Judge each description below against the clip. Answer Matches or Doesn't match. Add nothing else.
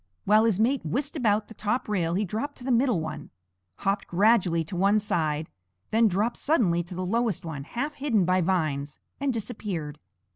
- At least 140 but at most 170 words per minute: Doesn't match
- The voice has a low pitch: Doesn't match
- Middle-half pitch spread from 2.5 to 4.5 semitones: Doesn't match